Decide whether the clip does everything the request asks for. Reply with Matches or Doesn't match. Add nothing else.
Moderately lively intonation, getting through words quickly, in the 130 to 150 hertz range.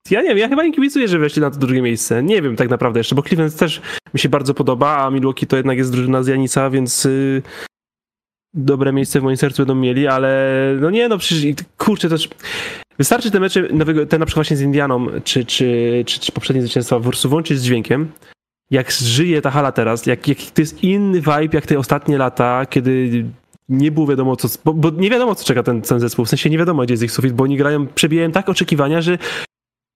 Matches